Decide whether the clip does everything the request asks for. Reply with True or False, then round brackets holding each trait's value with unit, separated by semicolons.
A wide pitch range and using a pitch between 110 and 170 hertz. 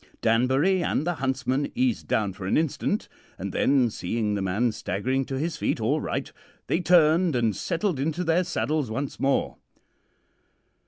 True (6.1 semitones; 135 Hz)